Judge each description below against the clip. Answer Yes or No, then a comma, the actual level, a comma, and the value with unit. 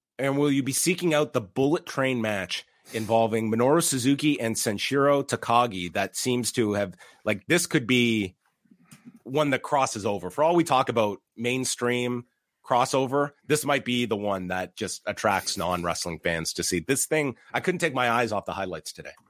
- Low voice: Yes, low, 125 Hz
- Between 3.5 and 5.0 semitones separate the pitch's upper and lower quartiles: Yes, average, 3.8 semitones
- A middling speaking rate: Yes, average, 185 wpm